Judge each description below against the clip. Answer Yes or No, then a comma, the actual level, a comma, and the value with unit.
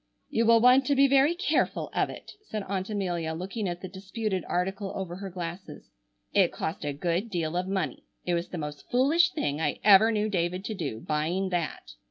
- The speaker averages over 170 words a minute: Yes, fast, 205 wpm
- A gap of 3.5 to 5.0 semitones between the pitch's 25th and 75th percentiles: Yes, average, 4.2 semitones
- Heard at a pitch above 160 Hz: Yes, high, 190 Hz